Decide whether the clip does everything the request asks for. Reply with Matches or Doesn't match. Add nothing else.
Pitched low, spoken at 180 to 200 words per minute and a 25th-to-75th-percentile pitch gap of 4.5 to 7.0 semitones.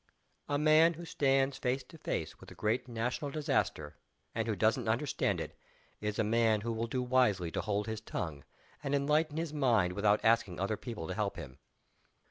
Matches